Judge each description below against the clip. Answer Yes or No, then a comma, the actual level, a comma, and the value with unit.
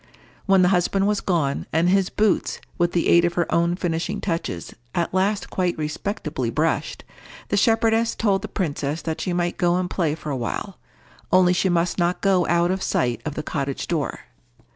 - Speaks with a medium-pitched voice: Yes, medium, 175 Hz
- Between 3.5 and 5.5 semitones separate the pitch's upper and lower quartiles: No, average, 2.7 semitones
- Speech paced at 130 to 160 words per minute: No, average, 190 wpm